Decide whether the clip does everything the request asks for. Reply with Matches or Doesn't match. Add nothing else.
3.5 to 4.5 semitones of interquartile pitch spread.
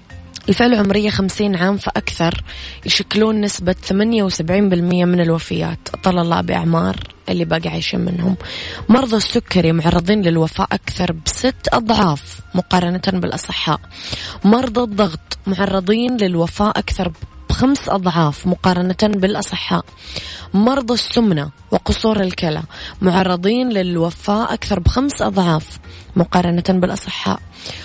Matches